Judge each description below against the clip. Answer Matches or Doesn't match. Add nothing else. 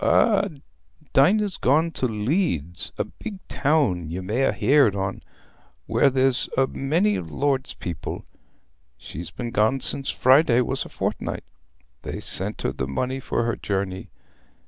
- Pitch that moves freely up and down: Matches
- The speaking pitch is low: Matches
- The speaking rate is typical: Matches